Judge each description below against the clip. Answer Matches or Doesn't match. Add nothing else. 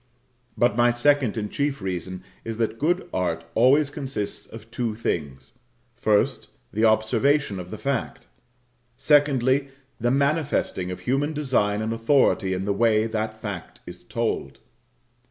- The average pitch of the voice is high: Doesn't match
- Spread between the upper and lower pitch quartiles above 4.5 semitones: Matches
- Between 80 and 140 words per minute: Matches